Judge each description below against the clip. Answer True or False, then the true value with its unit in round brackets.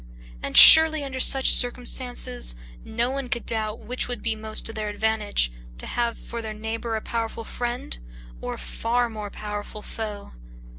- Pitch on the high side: True (225 Hz)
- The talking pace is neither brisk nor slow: True (165 wpm)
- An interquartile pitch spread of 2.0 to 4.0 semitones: True (2.4 semitones)